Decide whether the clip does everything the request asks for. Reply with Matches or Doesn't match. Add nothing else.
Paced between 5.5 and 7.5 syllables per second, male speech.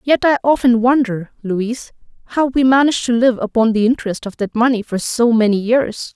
Doesn't match